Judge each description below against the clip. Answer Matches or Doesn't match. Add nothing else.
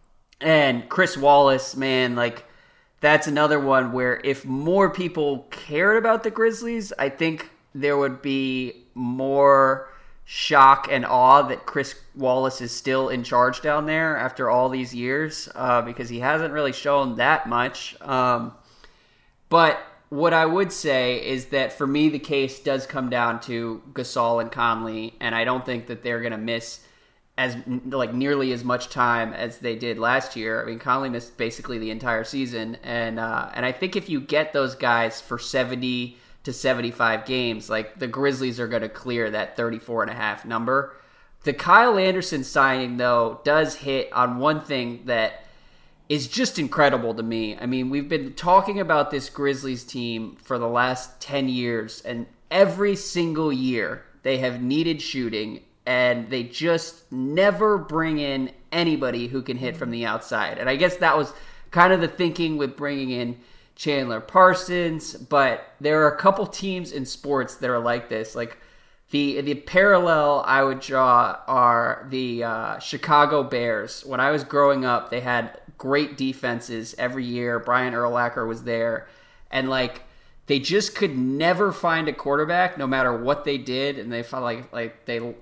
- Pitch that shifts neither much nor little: Matches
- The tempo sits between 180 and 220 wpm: Doesn't match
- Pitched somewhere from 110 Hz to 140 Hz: Matches